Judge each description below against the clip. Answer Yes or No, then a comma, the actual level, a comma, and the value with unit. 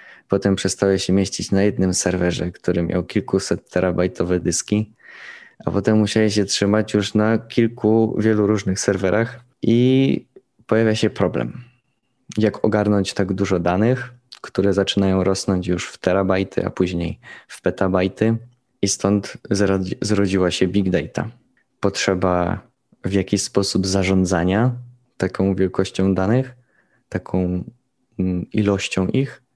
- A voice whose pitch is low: Yes, low, 100 Hz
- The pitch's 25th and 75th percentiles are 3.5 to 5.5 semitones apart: No, average, 2.8 semitones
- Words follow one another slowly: No, average, 120 wpm